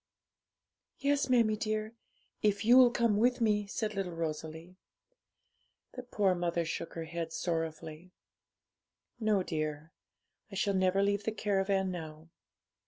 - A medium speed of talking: No, slow, 125 wpm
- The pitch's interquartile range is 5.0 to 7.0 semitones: No, average, 4.4 semitones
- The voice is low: No, high, 195 Hz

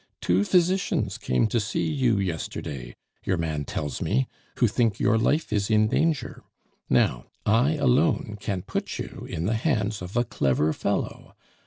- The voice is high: No, low, 105 Hz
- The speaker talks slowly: No, average, 160 wpm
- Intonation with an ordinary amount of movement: No, wide, 6.9 semitones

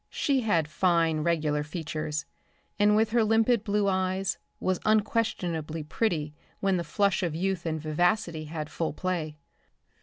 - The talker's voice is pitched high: No, medium, 175 Hz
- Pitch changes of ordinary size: Yes, average, 4.7 semitones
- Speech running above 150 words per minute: No, average, 145 wpm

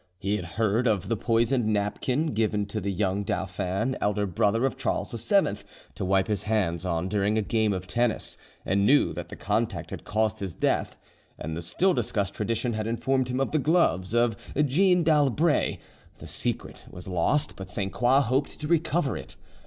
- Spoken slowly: No, average, 185 wpm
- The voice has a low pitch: Yes, low, 110 Hz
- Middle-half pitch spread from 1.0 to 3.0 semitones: No, average, 5.0 semitones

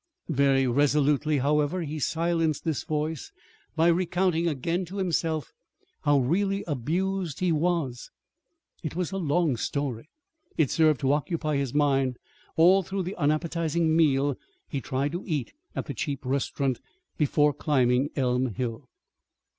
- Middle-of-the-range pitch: Yes, medium, 150 Hz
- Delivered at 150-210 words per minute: No, average, 140 wpm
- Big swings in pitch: No, average, 3.5 semitones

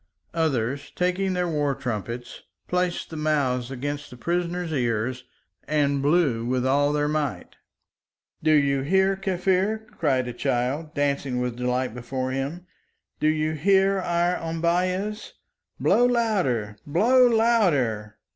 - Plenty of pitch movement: Yes, wide, 5.8 semitones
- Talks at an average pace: No, slow, 125 wpm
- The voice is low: No, medium, 150 Hz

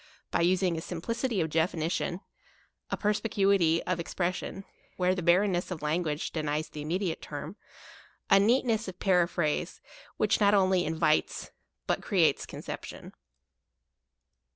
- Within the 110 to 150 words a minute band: Yes, average, 140 wpm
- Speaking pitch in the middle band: Yes, medium, 180 Hz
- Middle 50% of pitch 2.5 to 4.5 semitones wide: Yes, average, 3.2 semitones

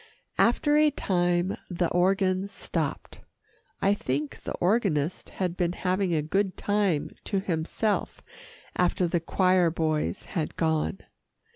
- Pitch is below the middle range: No, medium, 180 Hz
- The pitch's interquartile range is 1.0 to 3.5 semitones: Yes, average, 2.9 semitones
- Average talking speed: No, slow, 125 wpm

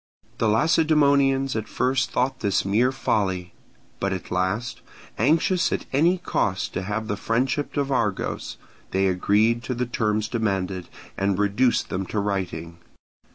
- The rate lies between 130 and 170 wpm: Yes, average, 145 wpm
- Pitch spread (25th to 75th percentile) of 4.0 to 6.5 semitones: Yes, average, 5.1 semitones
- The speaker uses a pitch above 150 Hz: No, low, 110 Hz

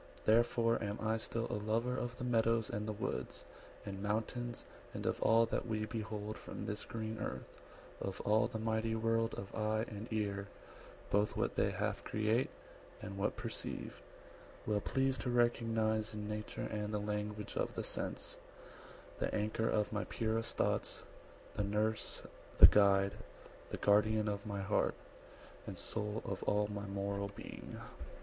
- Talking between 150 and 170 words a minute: Yes, average, 160 wpm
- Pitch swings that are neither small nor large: No, narrow, 1.6 semitones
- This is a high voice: No, low, 110 Hz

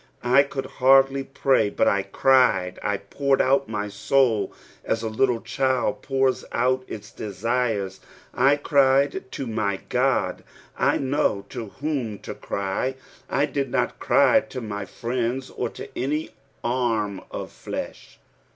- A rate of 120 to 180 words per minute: Yes, average, 140 wpm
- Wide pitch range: No, average, 4.2 semitones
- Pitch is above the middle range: No, low, 125 Hz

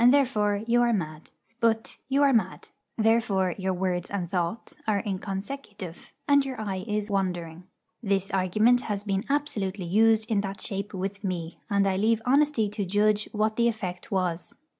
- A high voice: Yes, high, 205 Hz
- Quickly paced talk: No, average, 165 wpm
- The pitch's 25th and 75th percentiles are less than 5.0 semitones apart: Yes, average, 3.1 semitones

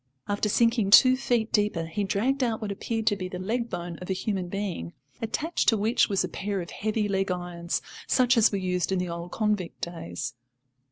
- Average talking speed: No, fast, 210 wpm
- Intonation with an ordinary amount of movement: Yes, average, 3.6 semitones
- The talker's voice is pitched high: Yes, high, 200 Hz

